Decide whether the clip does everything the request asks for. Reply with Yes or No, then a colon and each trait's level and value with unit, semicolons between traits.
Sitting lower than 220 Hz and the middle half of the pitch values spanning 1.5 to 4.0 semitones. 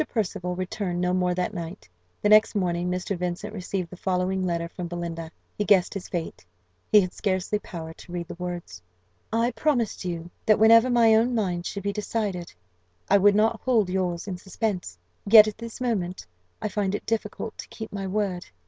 Yes: high, 190 Hz; average, 3.3 semitones